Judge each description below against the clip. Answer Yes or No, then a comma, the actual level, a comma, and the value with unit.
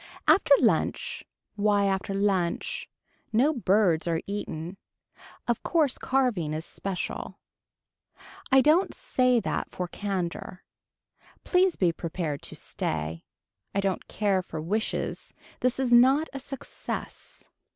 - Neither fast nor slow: No, slow, 120 wpm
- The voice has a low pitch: No, high, 200 Hz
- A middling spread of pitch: No, wide, 6.3 semitones